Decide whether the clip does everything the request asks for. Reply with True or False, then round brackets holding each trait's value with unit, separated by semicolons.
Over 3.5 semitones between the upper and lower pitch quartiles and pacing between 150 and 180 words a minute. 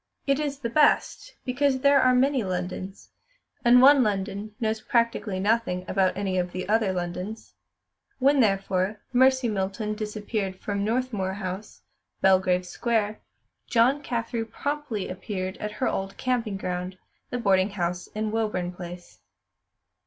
False (4.3 semitones; 140 wpm)